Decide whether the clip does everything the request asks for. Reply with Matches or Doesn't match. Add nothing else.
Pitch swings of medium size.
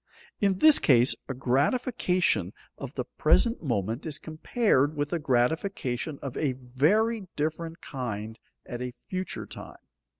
Doesn't match